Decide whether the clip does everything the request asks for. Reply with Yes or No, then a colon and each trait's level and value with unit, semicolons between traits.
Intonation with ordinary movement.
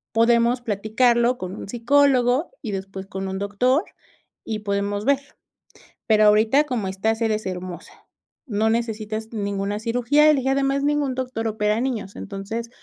Yes: average, 3.6 semitones